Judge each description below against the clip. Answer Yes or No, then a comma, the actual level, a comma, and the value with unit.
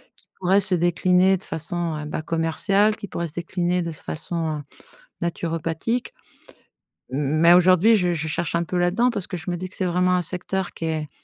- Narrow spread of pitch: Yes, narrow, 2.2 semitones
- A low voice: No, medium, 175 Hz